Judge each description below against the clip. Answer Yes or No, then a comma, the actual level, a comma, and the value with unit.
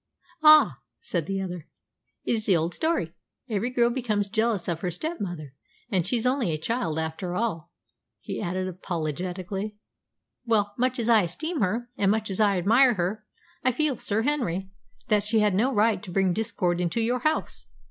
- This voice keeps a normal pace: Yes, average, 180 wpm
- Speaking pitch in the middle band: No, high, 205 Hz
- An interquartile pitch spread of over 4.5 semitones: Yes, average, 4.9 semitones